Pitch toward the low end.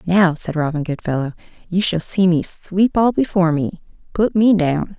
No: medium, 175 Hz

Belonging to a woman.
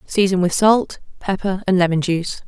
Yes: female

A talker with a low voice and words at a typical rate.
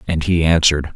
Yes: very low, 80 Hz; average, 190 wpm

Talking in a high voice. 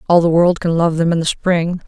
No: medium, 170 Hz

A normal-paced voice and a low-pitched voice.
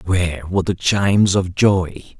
Yes: average, 165 wpm; very low, 90 Hz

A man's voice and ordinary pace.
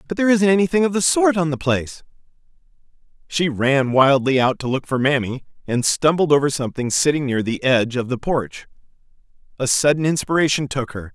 Yes: male; average, 185 wpm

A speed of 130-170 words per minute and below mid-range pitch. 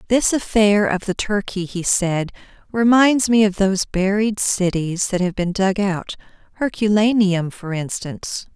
No: average, 140 wpm; high, 200 Hz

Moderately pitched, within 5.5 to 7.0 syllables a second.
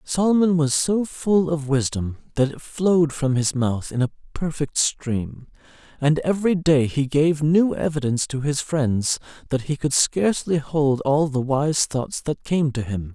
No: medium, 145 Hz; 4.3 syllables/s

